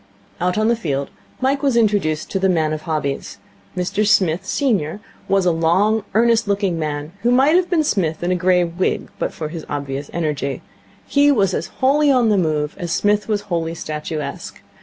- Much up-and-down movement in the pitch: Yes, wide, 5.7 semitones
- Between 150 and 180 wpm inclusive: No, average, 190 wpm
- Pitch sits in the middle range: Yes, medium, 180 Hz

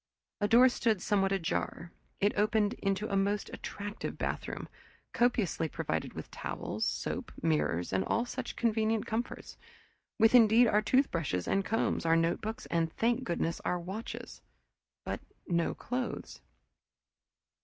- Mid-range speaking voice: No, high, 205 Hz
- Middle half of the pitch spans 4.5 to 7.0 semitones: Yes, average, 4.9 semitones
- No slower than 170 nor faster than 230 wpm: No, slow, 135 wpm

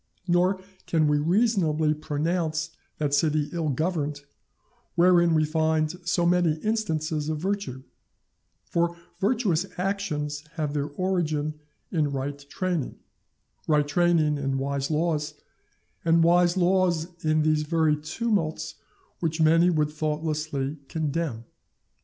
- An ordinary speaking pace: No, slow, 115 wpm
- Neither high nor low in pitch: Yes, medium, 155 Hz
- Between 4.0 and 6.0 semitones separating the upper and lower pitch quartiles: No, narrow, 2.5 semitones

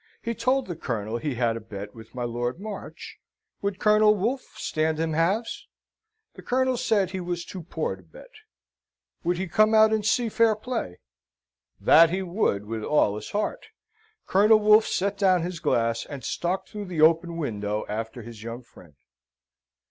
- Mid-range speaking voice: Yes, medium, 170 Hz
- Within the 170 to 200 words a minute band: Yes, average, 175 wpm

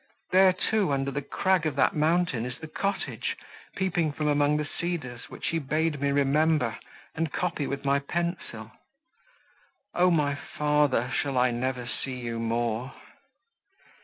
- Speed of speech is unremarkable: Yes, average, 150 wpm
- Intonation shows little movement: No, average, 4.2 semitones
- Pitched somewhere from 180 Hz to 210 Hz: No, medium, 145 Hz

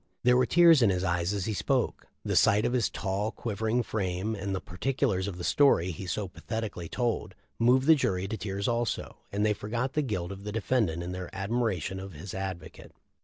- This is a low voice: Yes, low, 100 Hz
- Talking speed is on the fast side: Yes, fast, 215 wpm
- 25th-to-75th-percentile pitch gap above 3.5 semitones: Yes, average, 4.2 semitones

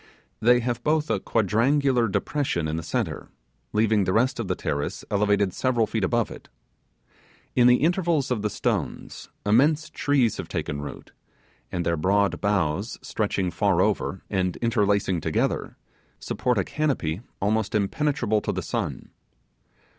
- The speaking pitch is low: Yes, low, 110 Hz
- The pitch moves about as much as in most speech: Yes, average, 4.5 semitones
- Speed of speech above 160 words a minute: No, average, 145 wpm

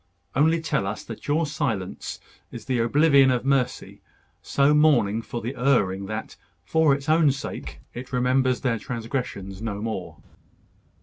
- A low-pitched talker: Yes, low, 125 Hz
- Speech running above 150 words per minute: No, average, 145 wpm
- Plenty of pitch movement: No, average, 4.1 semitones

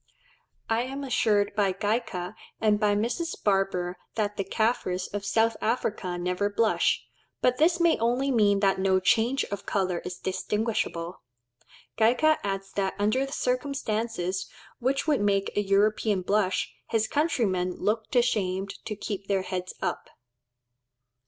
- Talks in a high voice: Yes, high, 205 Hz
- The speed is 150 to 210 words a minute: No, average, 140 wpm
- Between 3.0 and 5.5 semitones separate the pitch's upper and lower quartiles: Yes, average, 3.3 semitones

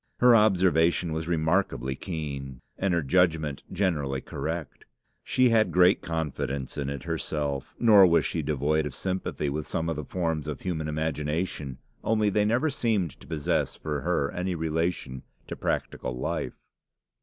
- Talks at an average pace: Yes, average, 155 wpm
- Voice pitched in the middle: No, very low, 80 Hz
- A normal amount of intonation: Yes, average, 4.0 semitones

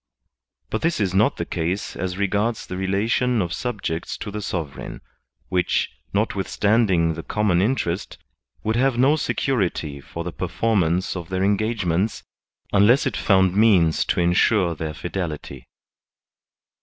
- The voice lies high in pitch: No, very low, 95 Hz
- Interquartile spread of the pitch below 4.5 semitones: Yes, average, 4.1 semitones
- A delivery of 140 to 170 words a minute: Yes, average, 145 wpm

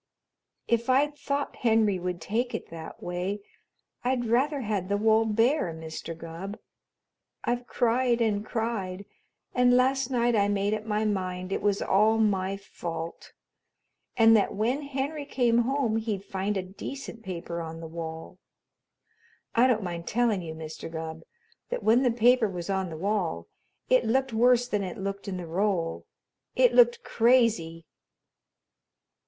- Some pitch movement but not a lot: Yes, average, 4.9 semitones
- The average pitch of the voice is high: Yes, high, 215 Hz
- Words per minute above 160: No, average, 155 wpm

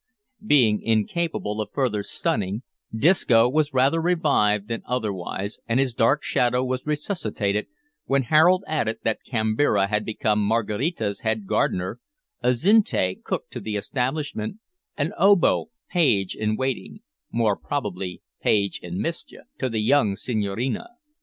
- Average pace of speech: No, slow, 130 wpm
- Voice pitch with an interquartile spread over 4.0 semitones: Yes, wide, 5.4 semitones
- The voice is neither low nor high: No, low, 115 Hz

